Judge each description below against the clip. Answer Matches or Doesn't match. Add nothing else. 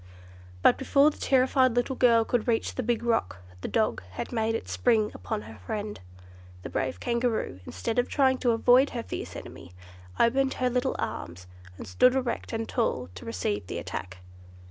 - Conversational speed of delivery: Matches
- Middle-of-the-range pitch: Doesn't match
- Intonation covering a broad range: Matches